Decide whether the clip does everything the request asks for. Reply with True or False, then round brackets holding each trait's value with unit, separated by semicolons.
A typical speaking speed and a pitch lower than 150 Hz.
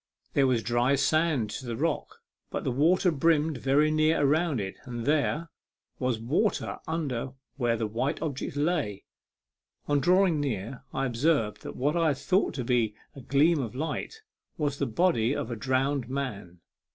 True (170 wpm; 140 Hz)